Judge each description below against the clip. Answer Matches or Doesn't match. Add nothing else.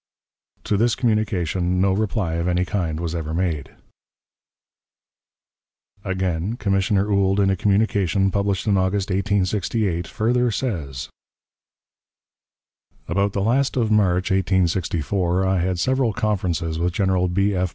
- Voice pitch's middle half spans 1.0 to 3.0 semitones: Matches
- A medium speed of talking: Doesn't match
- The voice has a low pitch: Matches